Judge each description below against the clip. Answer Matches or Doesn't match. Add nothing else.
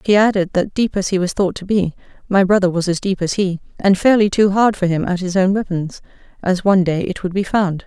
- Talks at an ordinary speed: Doesn't match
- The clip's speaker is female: Matches